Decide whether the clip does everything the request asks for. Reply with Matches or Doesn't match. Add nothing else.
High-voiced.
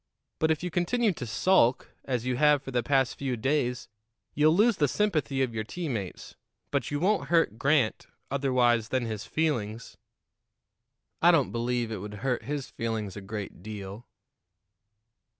Doesn't match